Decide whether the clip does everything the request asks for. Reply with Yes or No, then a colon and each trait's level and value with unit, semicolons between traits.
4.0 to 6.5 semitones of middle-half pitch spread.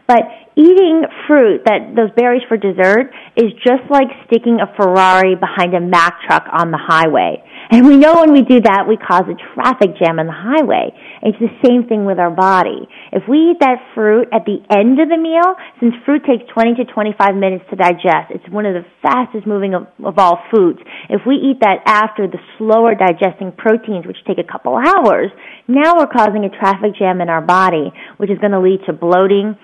Yes: average, 5.0 semitones